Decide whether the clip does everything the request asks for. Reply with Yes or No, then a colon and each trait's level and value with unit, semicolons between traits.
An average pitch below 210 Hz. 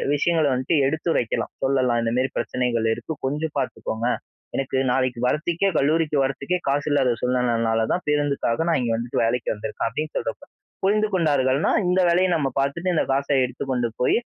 Yes: low, 135 Hz